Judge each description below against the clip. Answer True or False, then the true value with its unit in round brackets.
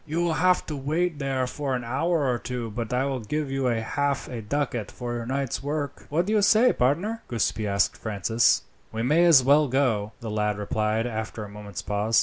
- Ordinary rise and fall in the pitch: True (4.8 semitones)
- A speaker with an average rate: False (210 wpm)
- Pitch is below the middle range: True (125 Hz)